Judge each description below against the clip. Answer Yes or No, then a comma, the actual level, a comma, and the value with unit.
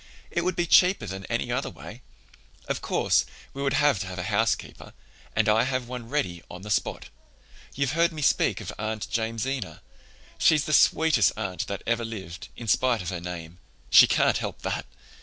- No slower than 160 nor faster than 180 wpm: No, average, 190 wpm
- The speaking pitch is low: Yes, low, 115 Hz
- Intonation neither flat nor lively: No, wide, 6.4 semitones